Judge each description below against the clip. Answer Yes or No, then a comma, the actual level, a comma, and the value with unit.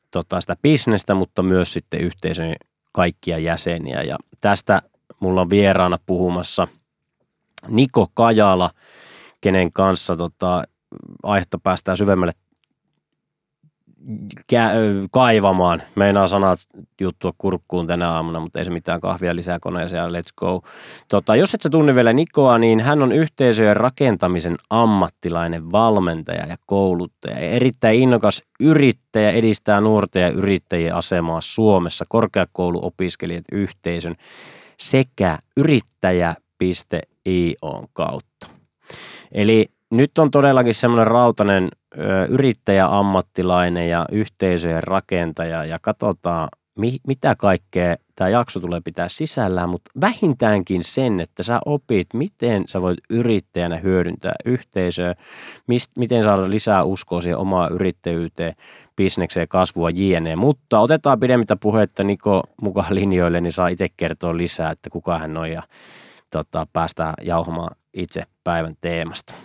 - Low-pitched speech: Yes, very low, 95 Hz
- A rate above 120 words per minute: No, average, 115 wpm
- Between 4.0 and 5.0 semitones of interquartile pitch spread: Yes, average, 4.6 semitones